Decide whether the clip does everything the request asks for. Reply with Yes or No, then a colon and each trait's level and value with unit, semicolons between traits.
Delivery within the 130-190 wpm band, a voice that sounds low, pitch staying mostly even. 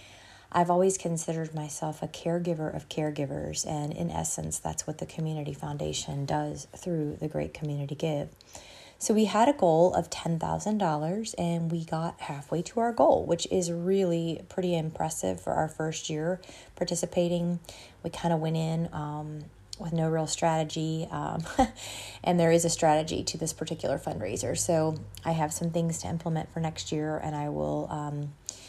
No: average, 170 wpm; medium, 160 Hz; narrow, 2.3 semitones